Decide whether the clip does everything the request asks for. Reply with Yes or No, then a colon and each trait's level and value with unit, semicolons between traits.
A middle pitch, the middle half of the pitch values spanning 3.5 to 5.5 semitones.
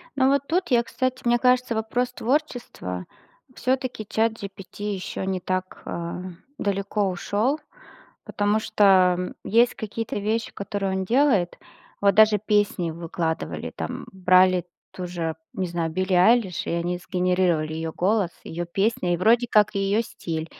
No: high, 200 Hz; average, 4.1 semitones